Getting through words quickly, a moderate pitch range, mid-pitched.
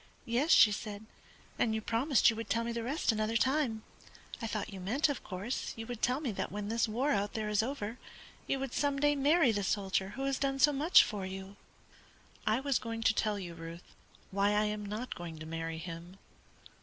No: fast, 215 wpm; average, 4.7 semitones; high, 220 Hz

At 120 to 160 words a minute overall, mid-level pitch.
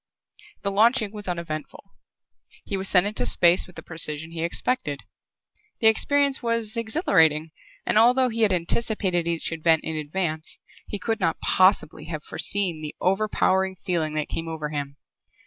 Yes: average, 155 wpm; medium, 180 Hz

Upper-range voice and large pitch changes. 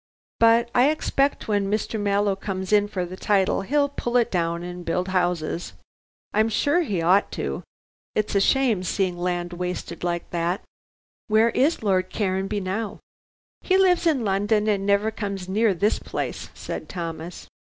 No: high, 200 Hz; average, 3.6 semitones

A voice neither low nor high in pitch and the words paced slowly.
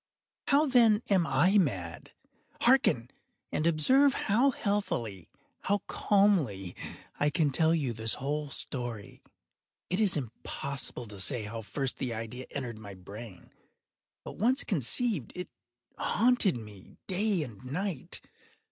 Yes: medium, 145 Hz; slow, 125 wpm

